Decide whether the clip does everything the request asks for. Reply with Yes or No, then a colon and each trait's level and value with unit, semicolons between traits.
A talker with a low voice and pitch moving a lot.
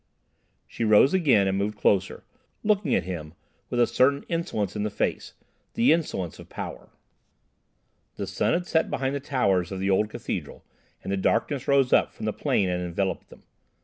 Yes: low, 105 Hz; wide, 6.5 semitones